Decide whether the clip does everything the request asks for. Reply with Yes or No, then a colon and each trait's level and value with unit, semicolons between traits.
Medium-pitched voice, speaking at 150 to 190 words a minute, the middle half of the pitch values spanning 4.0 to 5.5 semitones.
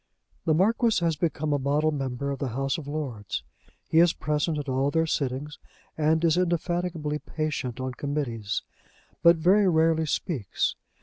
No: medium, 150 Hz; average, 160 wpm; average, 3.1 semitones